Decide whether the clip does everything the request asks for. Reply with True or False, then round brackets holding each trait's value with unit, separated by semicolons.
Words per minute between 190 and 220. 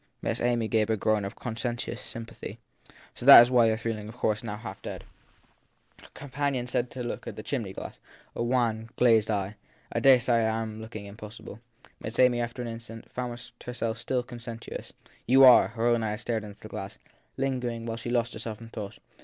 True (195 wpm)